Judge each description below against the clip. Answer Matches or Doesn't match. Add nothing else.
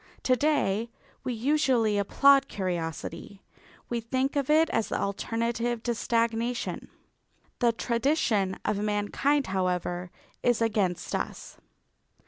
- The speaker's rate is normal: Doesn't match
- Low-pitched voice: Doesn't match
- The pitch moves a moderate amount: Matches